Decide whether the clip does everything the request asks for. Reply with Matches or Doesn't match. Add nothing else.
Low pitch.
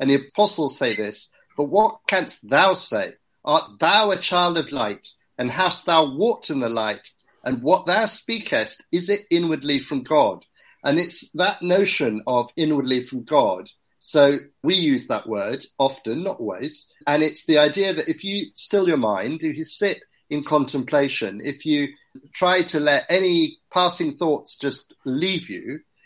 Doesn't match